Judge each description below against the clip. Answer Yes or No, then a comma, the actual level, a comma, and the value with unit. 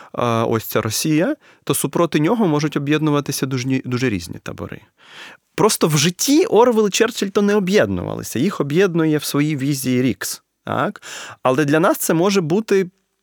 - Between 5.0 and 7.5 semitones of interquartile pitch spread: Yes, wide, 5.5 semitones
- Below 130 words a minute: No, average, 145 wpm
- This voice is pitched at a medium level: Yes, medium, 155 Hz